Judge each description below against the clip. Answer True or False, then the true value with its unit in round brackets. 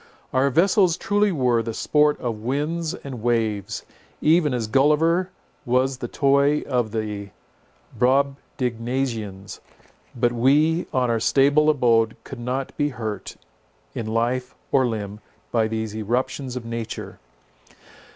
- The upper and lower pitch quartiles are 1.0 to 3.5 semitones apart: False (4.0 semitones)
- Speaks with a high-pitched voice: False (125 Hz)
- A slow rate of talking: True (125 wpm)